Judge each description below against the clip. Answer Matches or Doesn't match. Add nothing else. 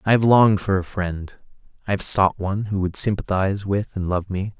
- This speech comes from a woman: Doesn't match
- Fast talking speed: Matches